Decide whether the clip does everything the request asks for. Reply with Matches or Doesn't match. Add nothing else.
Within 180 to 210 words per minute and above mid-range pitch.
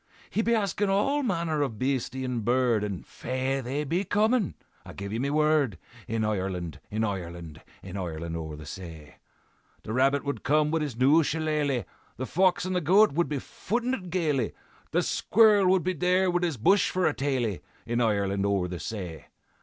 Doesn't match